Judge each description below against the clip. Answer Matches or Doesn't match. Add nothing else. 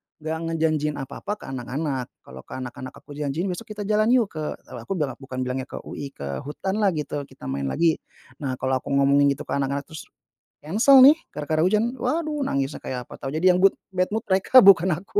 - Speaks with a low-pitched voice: Doesn't match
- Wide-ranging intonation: Matches